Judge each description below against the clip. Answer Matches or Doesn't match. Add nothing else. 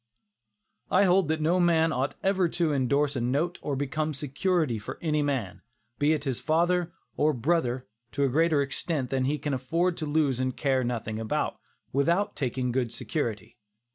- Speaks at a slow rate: Doesn't match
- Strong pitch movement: Doesn't match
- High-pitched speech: Doesn't match